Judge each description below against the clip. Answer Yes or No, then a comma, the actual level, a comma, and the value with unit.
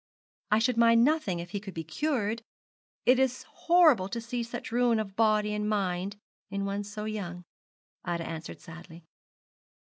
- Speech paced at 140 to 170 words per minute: Yes, average, 160 wpm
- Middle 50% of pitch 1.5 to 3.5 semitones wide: No, average, 4.0 semitones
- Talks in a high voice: Yes, high, 210 Hz